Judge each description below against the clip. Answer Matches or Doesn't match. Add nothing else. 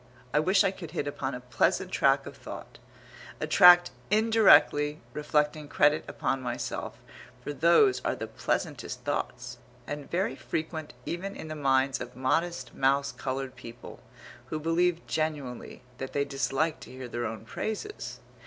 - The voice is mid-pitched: Matches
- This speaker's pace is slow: Doesn't match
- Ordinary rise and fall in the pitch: Matches